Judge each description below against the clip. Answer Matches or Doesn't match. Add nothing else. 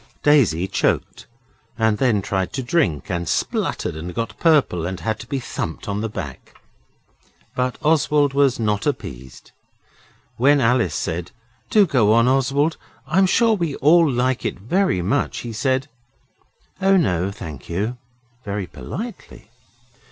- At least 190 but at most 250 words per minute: Doesn't match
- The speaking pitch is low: Matches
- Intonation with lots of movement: Matches